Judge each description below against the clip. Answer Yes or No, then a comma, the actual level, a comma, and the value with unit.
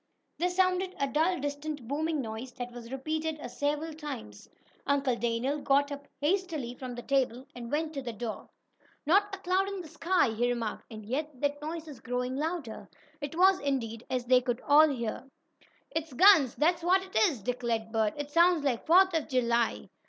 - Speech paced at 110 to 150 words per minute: No, average, 185 wpm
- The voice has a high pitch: Yes, very high, 285 Hz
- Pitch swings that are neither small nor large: Yes, average, 4.8 semitones